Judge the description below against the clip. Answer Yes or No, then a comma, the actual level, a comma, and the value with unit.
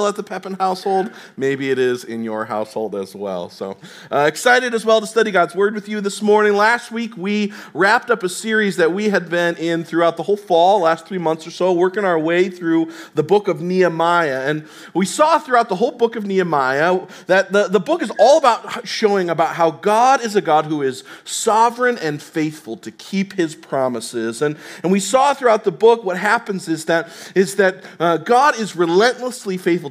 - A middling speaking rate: No, fast, 210 wpm